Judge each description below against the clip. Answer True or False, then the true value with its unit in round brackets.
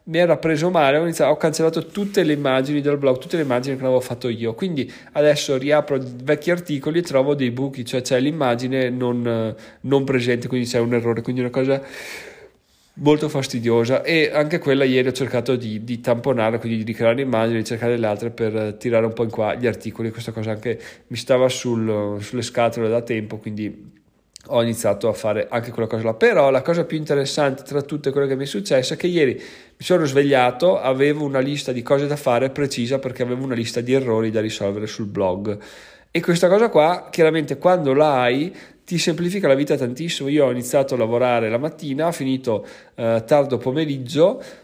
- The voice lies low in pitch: True (130 Hz)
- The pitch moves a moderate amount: True (4.0 semitones)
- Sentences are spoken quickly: True (200 wpm)